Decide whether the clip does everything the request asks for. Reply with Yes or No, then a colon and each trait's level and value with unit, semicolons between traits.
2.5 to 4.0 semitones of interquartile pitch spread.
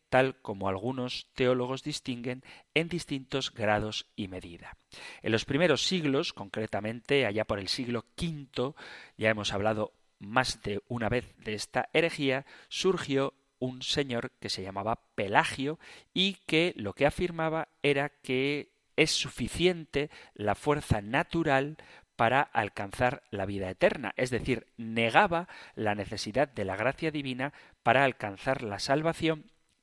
No: average, 5.2 semitones